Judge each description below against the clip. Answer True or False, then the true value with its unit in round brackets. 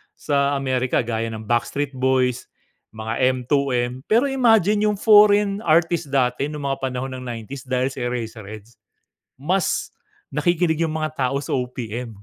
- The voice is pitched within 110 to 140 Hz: True (135 Hz)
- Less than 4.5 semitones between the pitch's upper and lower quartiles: False (4.9 semitones)